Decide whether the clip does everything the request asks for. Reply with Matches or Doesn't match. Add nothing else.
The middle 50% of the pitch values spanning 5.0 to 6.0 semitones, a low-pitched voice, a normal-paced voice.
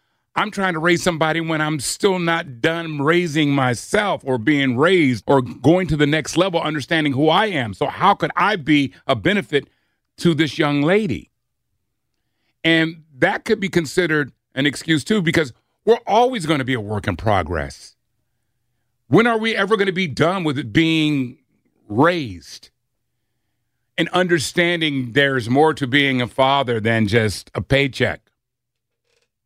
Doesn't match